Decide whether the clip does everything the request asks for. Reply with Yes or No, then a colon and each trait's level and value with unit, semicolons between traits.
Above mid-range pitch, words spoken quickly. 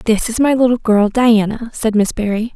Yes: high, 225 Hz; fast, 210 wpm